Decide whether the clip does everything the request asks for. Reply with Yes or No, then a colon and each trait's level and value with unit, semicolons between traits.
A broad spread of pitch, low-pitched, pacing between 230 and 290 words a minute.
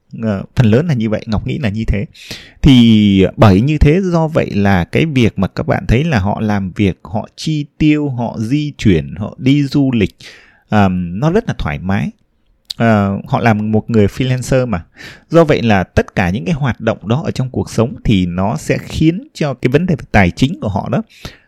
No: wide, 5.8 semitones; low, 115 Hz; average, 220 wpm